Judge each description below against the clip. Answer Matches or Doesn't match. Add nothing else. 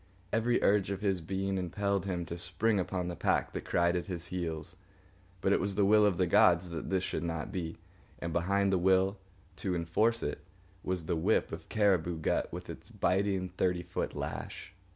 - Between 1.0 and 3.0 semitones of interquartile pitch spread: Matches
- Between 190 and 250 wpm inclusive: Matches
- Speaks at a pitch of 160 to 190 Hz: Doesn't match